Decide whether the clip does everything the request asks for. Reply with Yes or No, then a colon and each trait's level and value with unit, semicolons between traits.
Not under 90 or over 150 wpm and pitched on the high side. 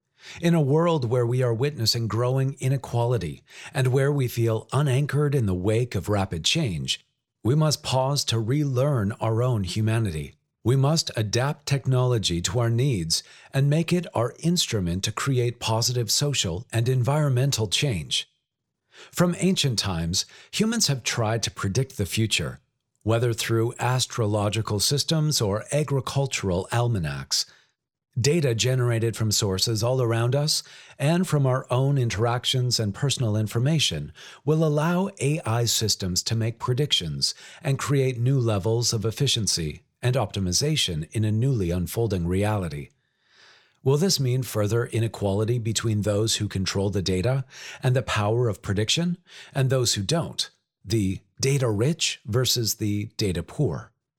No: average, 140 wpm; low, 120 Hz